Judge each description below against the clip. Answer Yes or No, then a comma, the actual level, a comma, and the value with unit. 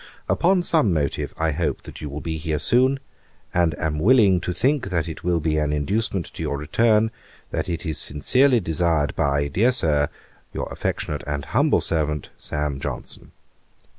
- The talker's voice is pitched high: No, very low, 80 Hz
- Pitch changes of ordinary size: No, wide, 6.7 semitones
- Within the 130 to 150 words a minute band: No, average, 165 wpm